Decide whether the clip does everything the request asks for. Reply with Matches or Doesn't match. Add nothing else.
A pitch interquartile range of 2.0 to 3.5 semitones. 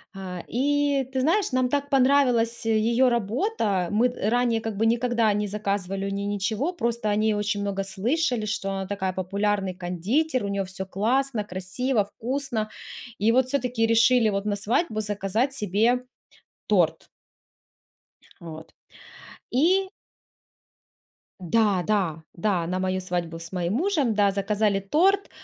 Doesn't match